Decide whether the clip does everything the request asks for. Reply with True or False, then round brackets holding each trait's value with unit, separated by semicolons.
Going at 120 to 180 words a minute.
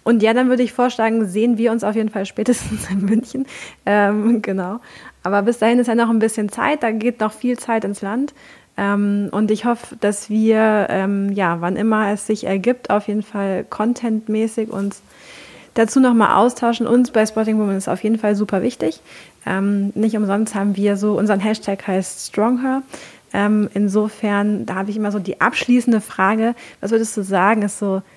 False (190 wpm)